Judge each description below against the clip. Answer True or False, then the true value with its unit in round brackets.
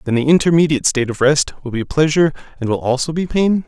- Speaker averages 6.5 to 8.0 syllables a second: True (6.9 syllables/s)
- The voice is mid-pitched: True (145 Hz)